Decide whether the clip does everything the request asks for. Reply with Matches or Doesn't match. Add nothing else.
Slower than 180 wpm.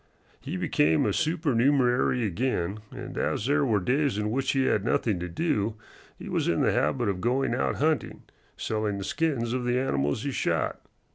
Doesn't match